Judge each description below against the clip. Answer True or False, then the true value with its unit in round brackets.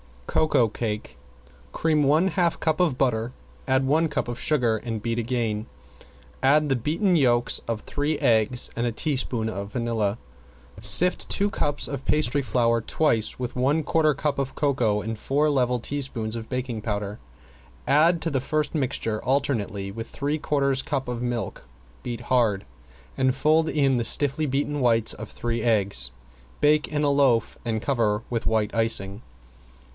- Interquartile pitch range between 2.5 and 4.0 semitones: False (4.4 semitones)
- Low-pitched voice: True (125 Hz)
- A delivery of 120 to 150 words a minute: False (160 wpm)